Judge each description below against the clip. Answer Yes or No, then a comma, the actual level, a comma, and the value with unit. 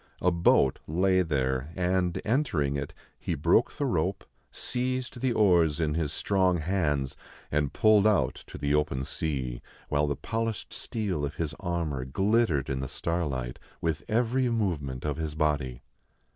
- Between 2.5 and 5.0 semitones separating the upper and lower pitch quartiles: No, wide, 5.4 semitones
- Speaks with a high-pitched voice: No, very low, 80 Hz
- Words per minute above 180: No, average, 155 wpm